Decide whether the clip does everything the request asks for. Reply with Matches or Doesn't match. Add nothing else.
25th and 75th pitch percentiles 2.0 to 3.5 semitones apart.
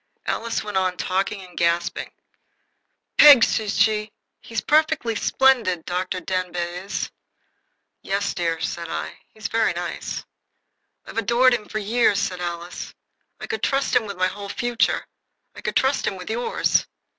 Doesn't match